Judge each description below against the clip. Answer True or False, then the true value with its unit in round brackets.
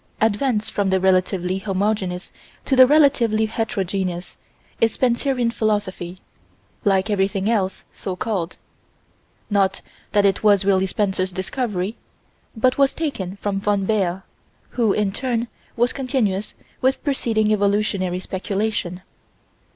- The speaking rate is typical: False (120 wpm)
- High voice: True (205 Hz)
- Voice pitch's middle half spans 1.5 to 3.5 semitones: True (3.2 semitones)